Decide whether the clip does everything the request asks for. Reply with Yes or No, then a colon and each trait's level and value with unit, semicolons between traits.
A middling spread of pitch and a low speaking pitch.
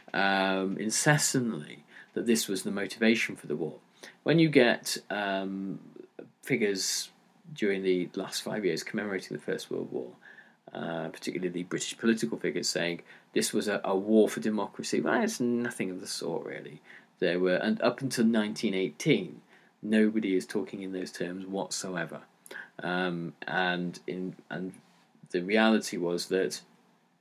Yes: average, 3.5 semitones; low, 100 Hz